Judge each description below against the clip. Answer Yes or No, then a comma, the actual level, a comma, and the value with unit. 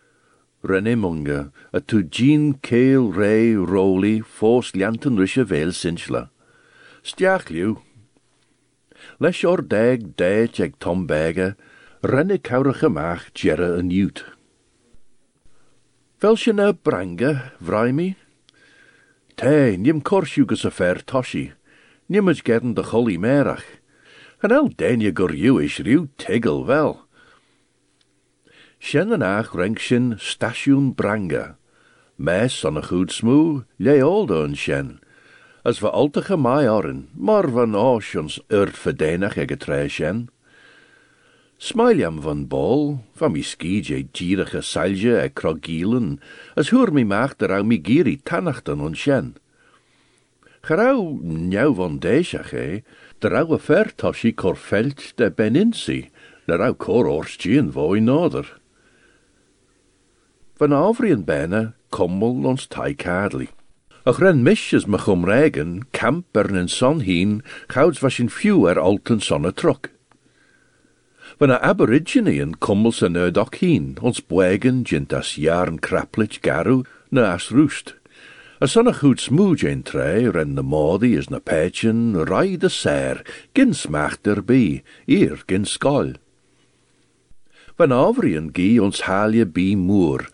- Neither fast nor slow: No, slow, 120 wpm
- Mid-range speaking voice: No, low, 115 Hz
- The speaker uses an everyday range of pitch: No, wide, 7.9 semitones